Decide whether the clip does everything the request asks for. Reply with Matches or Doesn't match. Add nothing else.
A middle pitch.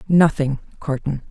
Matches